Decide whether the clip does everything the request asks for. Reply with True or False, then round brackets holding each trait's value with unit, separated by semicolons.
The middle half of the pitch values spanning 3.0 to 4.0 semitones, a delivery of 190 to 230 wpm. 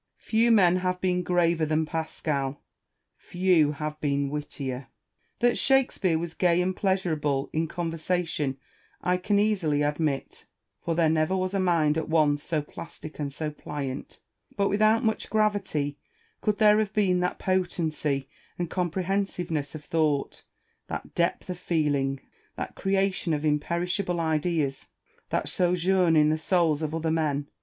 False (3.5 semitones; 145 wpm)